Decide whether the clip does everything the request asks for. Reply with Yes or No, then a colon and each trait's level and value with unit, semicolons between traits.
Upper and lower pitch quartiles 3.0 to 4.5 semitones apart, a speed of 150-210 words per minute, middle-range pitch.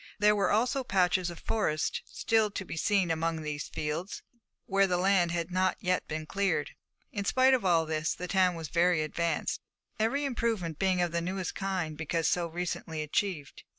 Yes: average, 3.4 semitones; average, 185 wpm; medium, 180 Hz